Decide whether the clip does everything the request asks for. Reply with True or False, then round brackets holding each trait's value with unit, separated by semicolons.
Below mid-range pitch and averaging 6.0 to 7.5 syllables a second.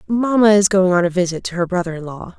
False (185 Hz; 6.3 syllables/s)